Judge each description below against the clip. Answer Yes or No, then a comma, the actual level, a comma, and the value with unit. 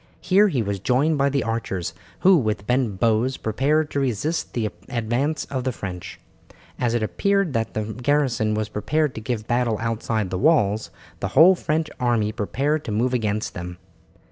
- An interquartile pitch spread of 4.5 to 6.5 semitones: Yes, average, 5.0 semitones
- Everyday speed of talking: Yes, average, 175 wpm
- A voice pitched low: Yes, low, 120 Hz